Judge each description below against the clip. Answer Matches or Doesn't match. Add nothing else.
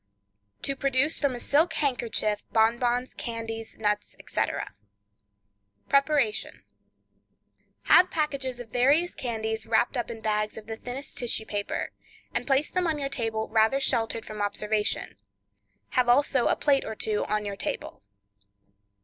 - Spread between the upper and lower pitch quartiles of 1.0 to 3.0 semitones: Doesn't match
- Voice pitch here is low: Doesn't match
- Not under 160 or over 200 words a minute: Doesn't match